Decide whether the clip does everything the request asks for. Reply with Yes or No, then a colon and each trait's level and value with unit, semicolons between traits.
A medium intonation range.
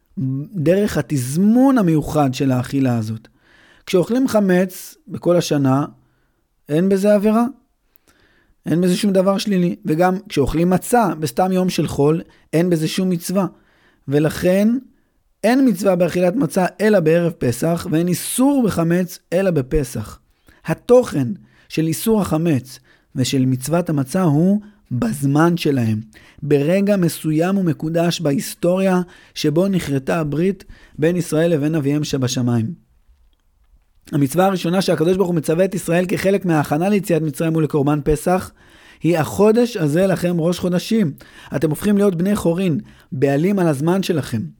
Yes: average, 4.3 semitones